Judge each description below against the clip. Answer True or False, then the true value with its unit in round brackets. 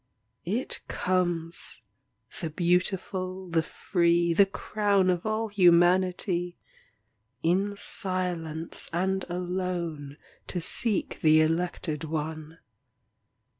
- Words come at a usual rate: False (90 wpm)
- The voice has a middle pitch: True (175 Hz)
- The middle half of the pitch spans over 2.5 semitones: False (2.2 semitones)